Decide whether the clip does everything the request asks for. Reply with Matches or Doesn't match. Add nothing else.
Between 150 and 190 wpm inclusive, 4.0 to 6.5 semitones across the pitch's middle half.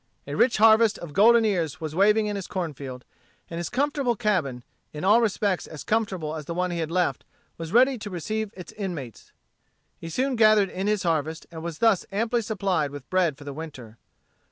Doesn't match